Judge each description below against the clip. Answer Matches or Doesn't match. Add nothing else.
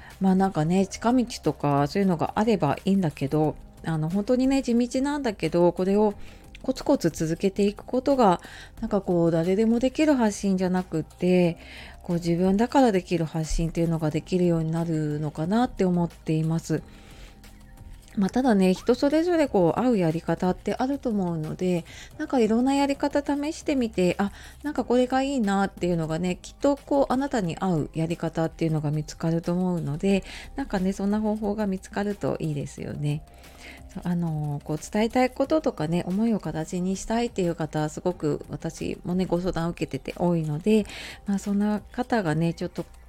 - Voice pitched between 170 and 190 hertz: Matches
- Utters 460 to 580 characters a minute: Doesn't match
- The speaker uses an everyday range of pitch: Doesn't match